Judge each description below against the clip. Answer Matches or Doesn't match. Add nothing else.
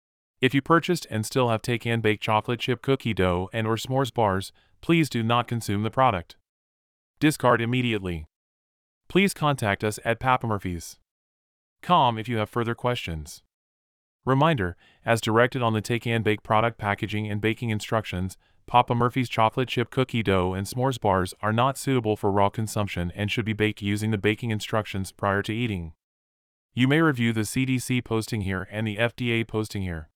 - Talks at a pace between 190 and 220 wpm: Doesn't match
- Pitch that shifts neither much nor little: Matches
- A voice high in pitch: Doesn't match